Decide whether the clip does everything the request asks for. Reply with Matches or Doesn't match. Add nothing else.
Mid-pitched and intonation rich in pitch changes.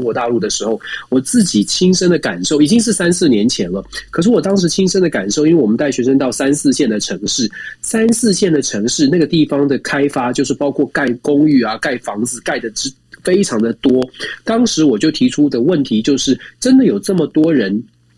Matches